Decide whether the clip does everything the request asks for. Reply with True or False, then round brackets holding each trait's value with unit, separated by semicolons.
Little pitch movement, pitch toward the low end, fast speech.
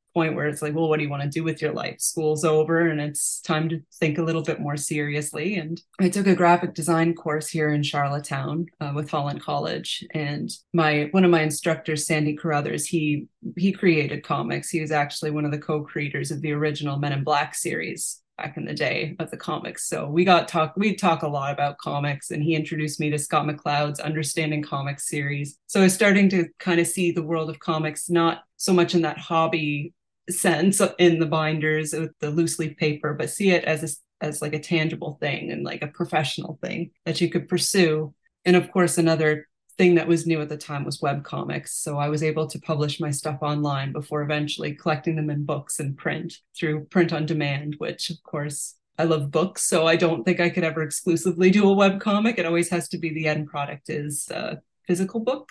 False (2.2 semitones; 160 Hz; 220 wpm)